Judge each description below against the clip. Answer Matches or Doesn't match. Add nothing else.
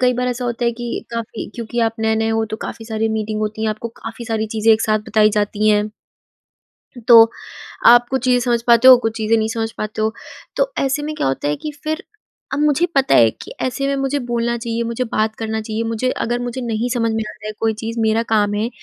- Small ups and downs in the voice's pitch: Matches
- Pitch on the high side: Matches